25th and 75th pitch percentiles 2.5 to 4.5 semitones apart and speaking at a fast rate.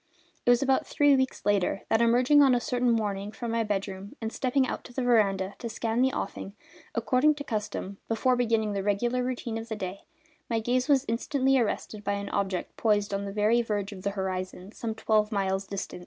Yes: average, 3.6 semitones; fast, 210 wpm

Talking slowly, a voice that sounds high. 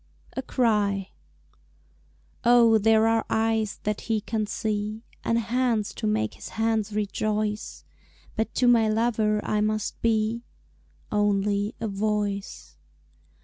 Yes: slow, 120 wpm; high, 215 Hz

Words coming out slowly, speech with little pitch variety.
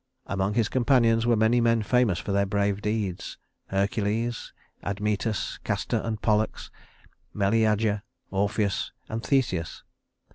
Yes: slow, 115 wpm; narrow, 2.2 semitones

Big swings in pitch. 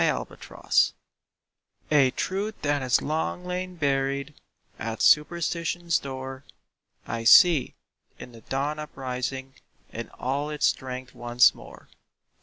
No: average, 3.4 semitones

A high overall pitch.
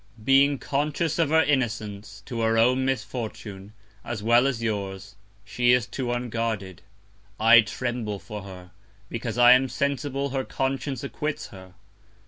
No: low, 120 Hz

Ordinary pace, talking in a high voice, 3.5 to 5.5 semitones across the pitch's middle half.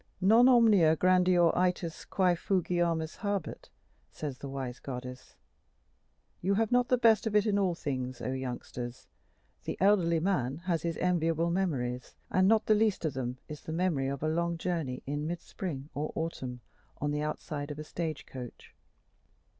No: average, 170 wpm; medium, 165 Hz; average, 5.1 semitones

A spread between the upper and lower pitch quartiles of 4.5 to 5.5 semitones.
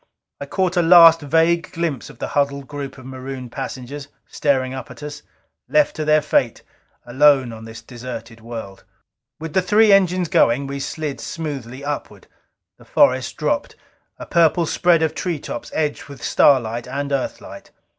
No: average, 4.1 semitones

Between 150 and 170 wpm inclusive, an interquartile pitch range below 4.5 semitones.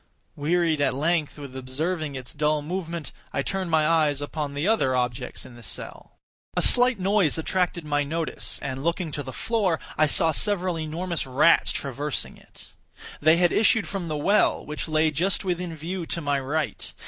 No: average, 180 wpm; average, 3.6 semitones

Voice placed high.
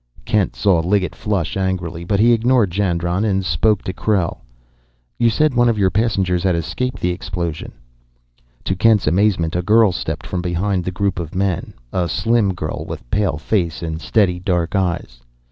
No: very low, 95 Hz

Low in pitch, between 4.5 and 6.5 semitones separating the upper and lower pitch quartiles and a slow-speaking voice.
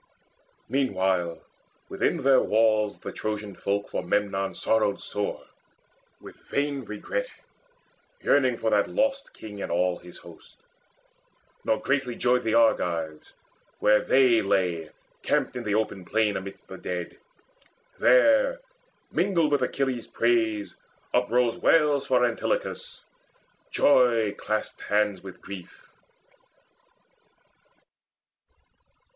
Yes: low, 110 Hz; average, 5.1 semitones; slow, 110 wpm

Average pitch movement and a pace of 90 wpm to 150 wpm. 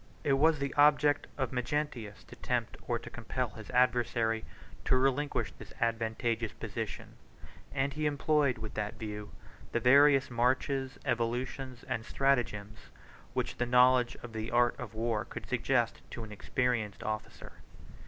Yes: average, 3.2 semitones; average, 145 wpm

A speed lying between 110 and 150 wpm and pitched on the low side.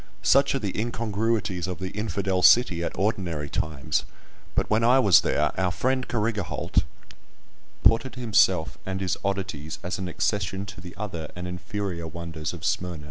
No: average, 165 wpm; very low, 95 Hz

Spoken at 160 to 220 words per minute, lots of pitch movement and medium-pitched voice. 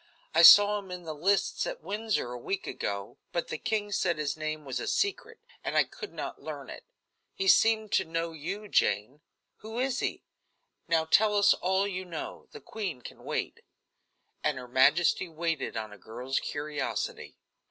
Yes: average, 180 wpm; wide, 5.7 semitones; medium, 175 Hz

